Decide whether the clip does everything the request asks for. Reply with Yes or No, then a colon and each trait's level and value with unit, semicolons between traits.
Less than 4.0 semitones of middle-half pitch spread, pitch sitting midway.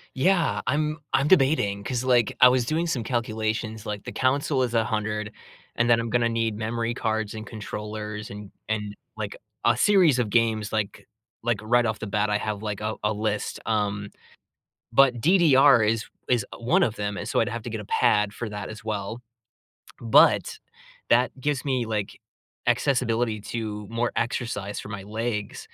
No: narrow, 2.6 semitones; low, 115 Hz